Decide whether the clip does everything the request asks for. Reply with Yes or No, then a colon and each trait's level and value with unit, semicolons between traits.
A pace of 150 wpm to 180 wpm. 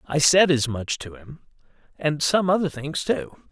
Yes: average, 170 wpm